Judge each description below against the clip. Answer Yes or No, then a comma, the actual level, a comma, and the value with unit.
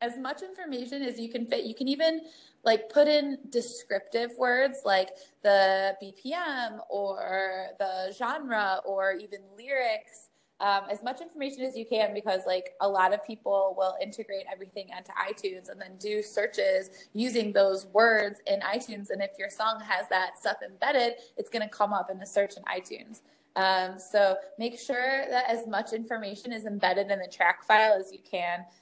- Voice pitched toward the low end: No, high, 215 Hz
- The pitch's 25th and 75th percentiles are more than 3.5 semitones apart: Yes, average, 4.1 semitones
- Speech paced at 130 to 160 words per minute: No, average, 180 wpm